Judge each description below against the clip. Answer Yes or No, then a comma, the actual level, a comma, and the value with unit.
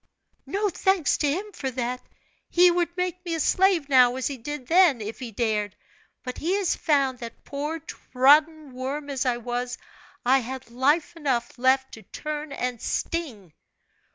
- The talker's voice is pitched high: Yes, very high, 275 Hz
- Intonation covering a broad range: No, average, 4.7 semitones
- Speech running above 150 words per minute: Yes, average, 170 wpm